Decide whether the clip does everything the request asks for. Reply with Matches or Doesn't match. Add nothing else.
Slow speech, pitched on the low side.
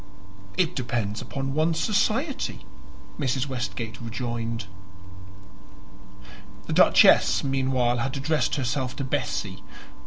Matches